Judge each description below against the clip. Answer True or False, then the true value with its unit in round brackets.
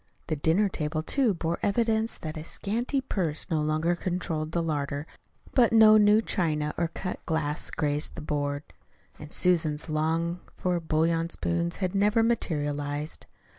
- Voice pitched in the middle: True (165 Hz)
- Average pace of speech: True (150 wpm)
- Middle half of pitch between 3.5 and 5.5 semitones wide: True (4.3 semitones)